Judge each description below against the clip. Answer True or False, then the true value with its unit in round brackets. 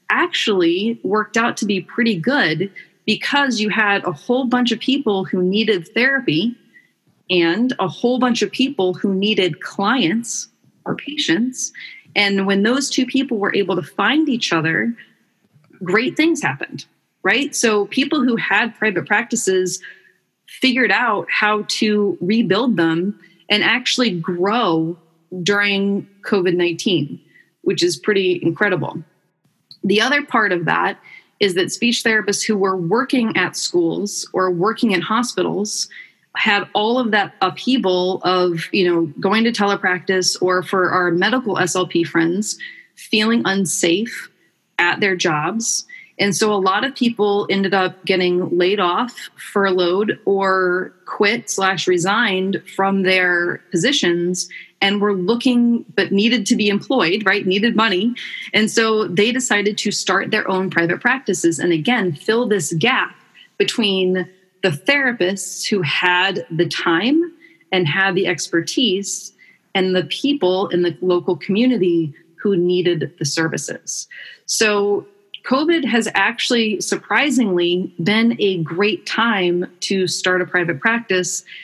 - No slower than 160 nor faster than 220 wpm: False (135 wpm)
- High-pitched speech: True (200 Hz)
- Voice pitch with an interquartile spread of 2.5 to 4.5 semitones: True (4.1 semitones)